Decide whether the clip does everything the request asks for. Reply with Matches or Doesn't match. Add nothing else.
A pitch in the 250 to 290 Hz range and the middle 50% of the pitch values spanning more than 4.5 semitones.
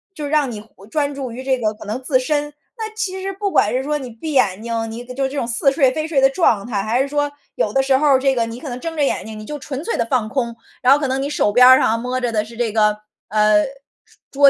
Doesn't match